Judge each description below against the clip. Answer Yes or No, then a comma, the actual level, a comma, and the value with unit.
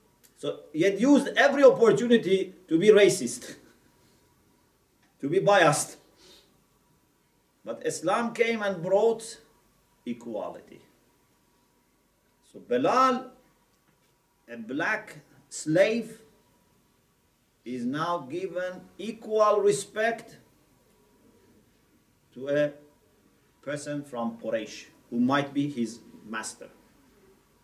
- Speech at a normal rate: No, slow, 85 wpm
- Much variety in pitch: Yes, wide, 8.1 semitones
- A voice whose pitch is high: Yes, high, 200 Hz